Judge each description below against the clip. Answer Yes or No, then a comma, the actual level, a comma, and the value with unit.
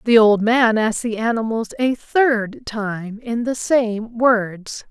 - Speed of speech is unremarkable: Yes, average, 160 wpm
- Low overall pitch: No, high, 225 Hz